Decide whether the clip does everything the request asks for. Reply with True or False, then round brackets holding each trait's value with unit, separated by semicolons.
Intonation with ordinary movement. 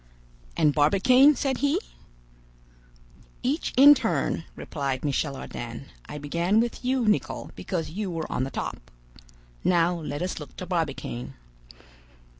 False (8.5 semitones)